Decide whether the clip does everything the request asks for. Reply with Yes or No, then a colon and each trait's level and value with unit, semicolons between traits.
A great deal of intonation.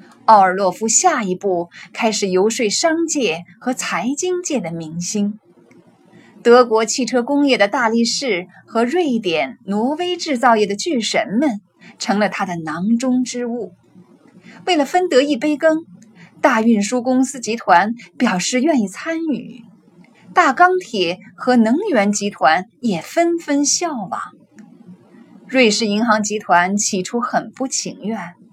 No: average, 4.7 semitones